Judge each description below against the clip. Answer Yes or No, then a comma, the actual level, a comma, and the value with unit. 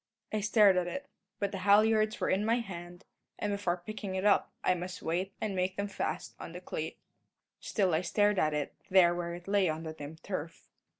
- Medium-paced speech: No, fast, 215 wpm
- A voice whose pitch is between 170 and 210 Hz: Yes, medium, 185 Hz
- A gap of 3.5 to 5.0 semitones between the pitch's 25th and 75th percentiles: No, average, 2.8 semitones